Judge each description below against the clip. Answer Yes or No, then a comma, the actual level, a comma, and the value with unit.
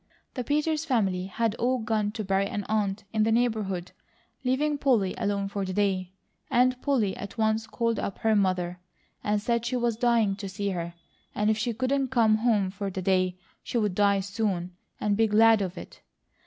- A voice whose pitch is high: Yes, high, 215 Hz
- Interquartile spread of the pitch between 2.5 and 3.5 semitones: Yes, average, 3.2 semitones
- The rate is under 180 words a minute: No, average, 195 wpm